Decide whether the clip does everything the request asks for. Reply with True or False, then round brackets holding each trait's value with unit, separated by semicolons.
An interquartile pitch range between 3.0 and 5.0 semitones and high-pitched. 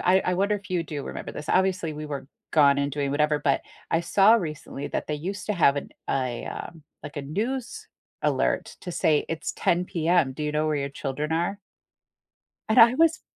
False (4.6 semitones; 160 Hz)